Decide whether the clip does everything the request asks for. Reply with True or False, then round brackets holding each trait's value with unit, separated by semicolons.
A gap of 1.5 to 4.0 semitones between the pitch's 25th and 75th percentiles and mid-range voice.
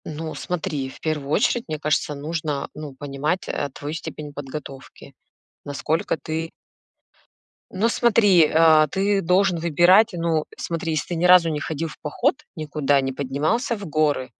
True (3.3 semitones; 155 Hz)